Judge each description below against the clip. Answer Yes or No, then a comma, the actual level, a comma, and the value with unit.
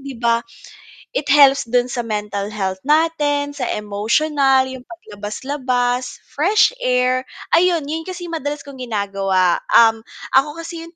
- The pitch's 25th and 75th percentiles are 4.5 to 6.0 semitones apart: Yes, average, 4.8 semitones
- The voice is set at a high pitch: Yes, very high, 260 Hz